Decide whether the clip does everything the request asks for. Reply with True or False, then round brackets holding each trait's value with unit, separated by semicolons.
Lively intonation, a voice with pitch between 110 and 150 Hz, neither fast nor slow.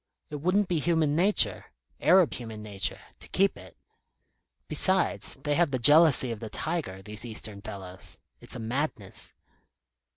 True (8.0 semitones; 135 Hz; 150 wpm)